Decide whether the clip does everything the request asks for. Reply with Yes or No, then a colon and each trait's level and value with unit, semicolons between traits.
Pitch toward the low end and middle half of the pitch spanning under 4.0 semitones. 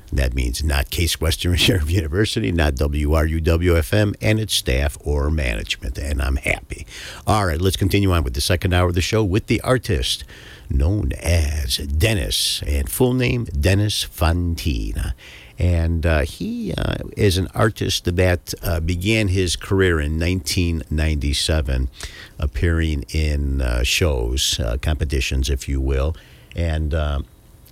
No: very low, 85 Hz; average, 4.8 semitones